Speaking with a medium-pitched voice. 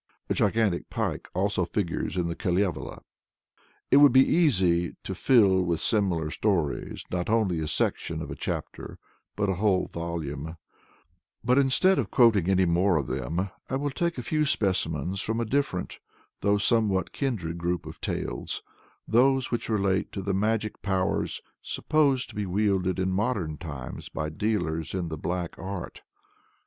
No: very low, 95 Hz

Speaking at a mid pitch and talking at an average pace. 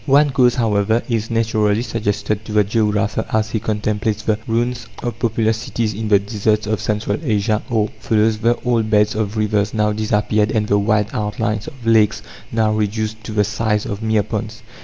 No: low, 110 Hz; average, 185 wpm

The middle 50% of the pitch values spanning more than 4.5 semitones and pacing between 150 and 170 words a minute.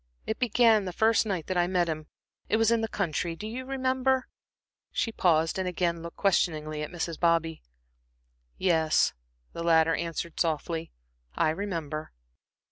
Yes: average, 5.1 semitones; average, 155 wpm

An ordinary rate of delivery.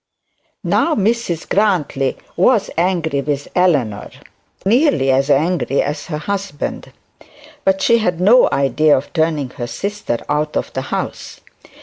No: slow, 130 wpm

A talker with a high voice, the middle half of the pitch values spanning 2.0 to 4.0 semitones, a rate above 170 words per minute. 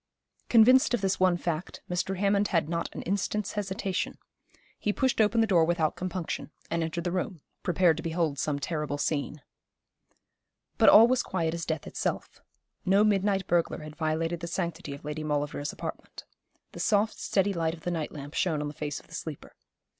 No: medium, 170 Hz; average, 3.7 semitones; average, 185 wpm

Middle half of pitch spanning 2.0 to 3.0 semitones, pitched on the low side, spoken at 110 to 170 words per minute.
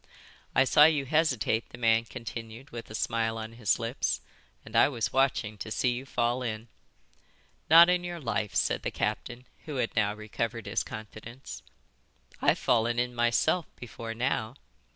Yes: average, 2.7 semitones; low, 120 Hz; average, 165 wpm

